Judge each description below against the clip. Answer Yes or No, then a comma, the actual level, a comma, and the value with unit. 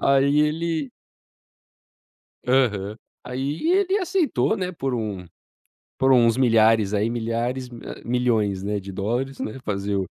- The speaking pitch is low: Yes, low, 125 Hz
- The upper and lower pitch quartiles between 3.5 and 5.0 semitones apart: Yes, average, 4.4 semitones